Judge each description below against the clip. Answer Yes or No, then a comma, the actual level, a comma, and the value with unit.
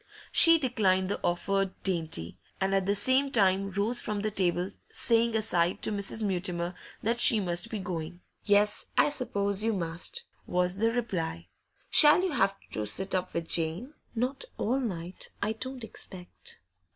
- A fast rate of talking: No, average, 165 wpm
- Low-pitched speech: No, high, 195 Hz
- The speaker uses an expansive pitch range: No, average, 4.1 semitones